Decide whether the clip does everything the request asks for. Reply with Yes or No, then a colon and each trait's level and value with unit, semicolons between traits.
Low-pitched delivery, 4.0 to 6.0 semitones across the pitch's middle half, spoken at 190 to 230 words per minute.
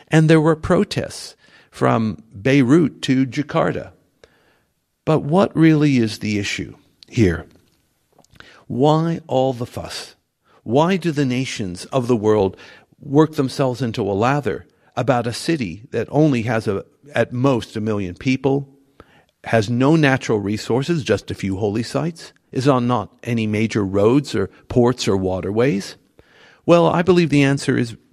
No: low, 130 Hz; average, 4.7 semitones; average, 145 wpm